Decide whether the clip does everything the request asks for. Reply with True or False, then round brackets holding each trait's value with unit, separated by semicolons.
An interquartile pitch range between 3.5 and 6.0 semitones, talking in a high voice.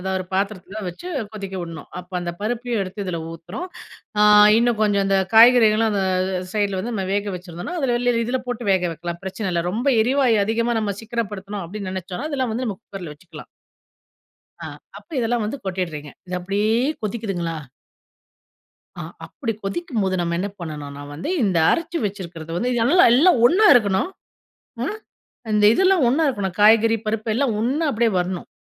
True (4.4 semitones; 210 Hz)